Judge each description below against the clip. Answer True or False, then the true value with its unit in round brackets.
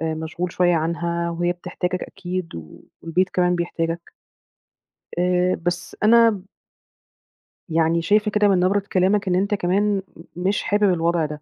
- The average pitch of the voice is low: False (180 Hz)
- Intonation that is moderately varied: False (2.3 semitones)